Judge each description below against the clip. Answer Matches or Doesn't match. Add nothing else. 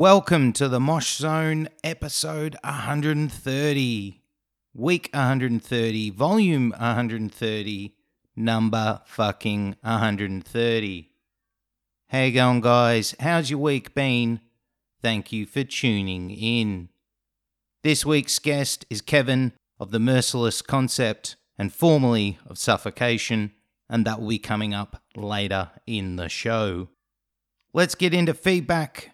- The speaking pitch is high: Doesn't match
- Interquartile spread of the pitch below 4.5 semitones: Doesn't match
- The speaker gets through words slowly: Matches